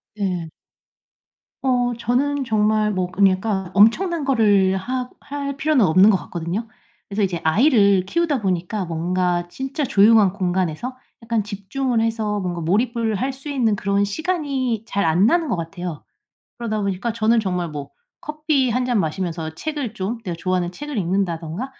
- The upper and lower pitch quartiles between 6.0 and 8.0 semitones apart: No, wide, 5.5 semitones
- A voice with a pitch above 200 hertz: Yes, high, 210 Hz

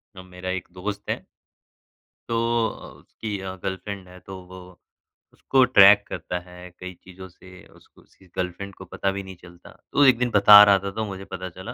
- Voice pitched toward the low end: Yes, very low, 95 Hz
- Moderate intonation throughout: No, narrow, 1.9 semitones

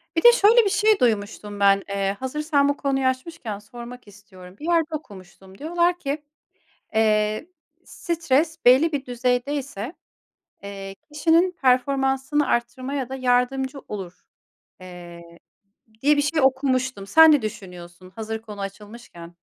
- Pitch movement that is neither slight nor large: No, wide, 6.3 semitones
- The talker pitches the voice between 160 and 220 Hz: No, very high, 255 Hz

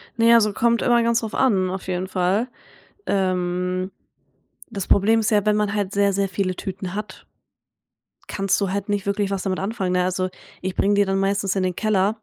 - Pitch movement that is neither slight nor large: No, narrow, 2.1 semitones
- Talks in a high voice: Yes, high, 195 Hz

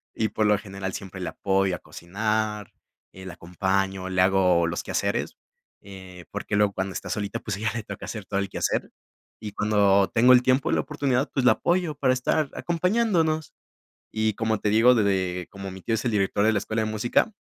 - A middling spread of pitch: Yes, average, 3.6 semitones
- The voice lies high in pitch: No, low, 105 Hz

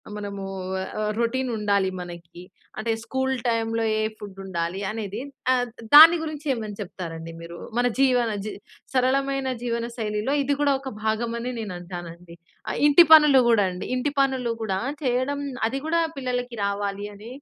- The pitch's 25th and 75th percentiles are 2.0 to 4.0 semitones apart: No, average, 4.6 semitones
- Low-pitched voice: No, high, 230 Hz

